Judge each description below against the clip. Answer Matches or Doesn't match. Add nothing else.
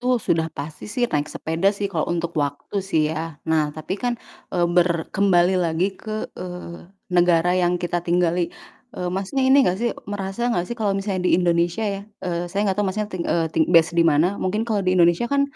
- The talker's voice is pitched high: Doesn't match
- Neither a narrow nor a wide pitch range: Matches